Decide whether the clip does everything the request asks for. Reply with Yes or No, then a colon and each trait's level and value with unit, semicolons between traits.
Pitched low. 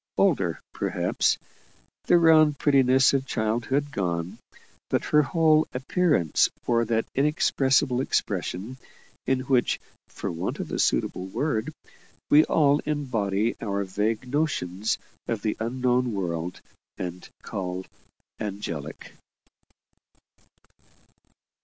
Yes: low, 120 Hz